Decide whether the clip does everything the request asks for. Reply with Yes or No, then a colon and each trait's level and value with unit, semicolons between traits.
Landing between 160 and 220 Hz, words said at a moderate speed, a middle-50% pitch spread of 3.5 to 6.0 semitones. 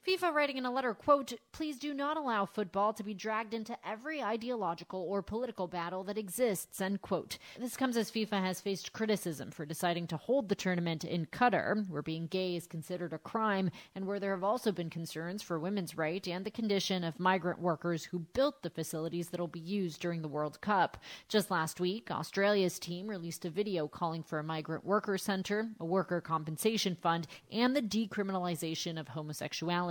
Yes: medium, 185 Hz; average, 195 wpm; average, 4.2 semitones